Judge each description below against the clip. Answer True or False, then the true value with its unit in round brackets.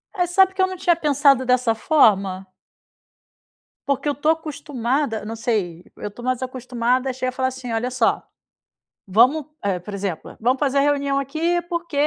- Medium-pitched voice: False (260 Hz)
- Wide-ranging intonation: False (4.2 semitones)